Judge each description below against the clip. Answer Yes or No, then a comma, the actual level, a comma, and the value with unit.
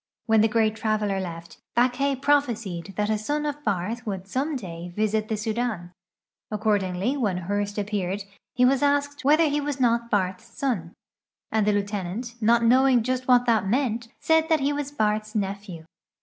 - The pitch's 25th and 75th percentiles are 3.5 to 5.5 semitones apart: Yes, average, 4.3 semitones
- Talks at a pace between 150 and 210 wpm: Yes, average, 175 wpm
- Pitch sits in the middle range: No, high, 220 Hz